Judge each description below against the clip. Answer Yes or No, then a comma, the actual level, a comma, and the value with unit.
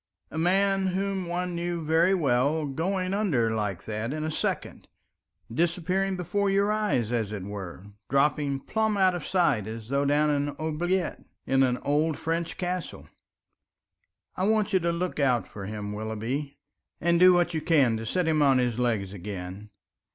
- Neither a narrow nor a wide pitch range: No, wide, 7.2 semitones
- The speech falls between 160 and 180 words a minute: Yes, average, 170 wpm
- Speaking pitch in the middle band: Yes, medium, 155 Hz